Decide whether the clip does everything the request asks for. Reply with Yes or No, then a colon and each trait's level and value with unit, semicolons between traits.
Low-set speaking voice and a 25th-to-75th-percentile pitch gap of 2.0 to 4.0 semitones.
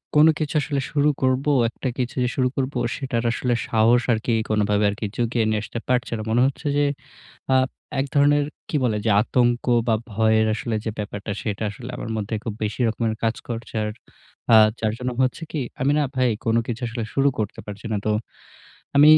Yes: low, 120 Hz; average, 3.1 semitones